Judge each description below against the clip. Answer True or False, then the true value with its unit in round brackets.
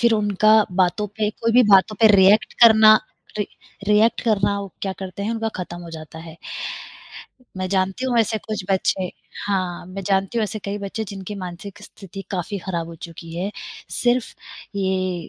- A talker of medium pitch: False (195 Hz)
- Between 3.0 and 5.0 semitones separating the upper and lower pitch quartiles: False (2.6 semitones)